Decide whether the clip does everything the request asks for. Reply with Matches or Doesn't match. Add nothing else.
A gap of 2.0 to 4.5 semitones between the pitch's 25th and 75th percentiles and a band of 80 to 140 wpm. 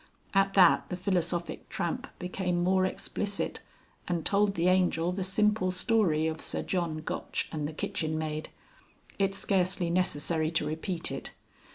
Doesn't match